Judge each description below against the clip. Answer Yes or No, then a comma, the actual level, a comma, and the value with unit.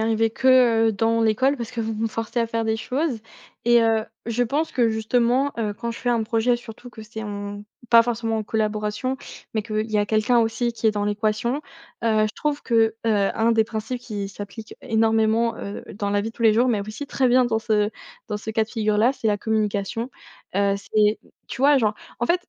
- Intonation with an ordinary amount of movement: No, narrow, 1.8 semitones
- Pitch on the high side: Yes, high, 225 Hz